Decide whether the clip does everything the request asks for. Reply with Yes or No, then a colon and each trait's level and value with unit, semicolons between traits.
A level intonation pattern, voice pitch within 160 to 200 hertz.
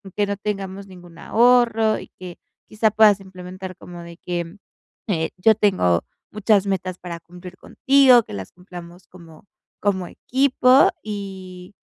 No: average, 3.1 semitones; high, 190 Hz